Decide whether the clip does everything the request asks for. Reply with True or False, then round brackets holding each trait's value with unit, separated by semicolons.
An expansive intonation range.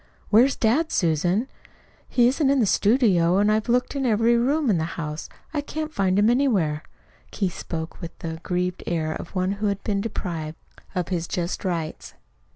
True (5.9 semitones)